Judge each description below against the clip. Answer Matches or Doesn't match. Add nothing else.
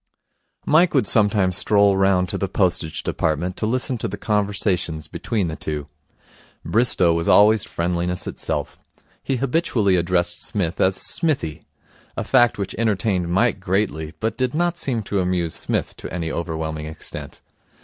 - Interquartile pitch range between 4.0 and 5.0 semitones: Matches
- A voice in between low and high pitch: Doesn't match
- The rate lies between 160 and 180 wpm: Doesn't match